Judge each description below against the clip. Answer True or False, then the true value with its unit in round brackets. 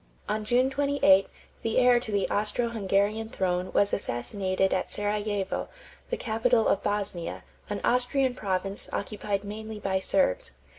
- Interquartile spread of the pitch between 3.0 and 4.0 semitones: False (2.6 semitones)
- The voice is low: False (205 Hz)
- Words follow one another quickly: False (140 wpm)